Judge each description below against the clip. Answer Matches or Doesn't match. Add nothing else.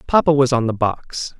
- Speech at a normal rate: Doesn't match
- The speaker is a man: Matches